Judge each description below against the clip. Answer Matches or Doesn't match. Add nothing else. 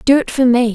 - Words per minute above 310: Matches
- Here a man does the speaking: Doesn't match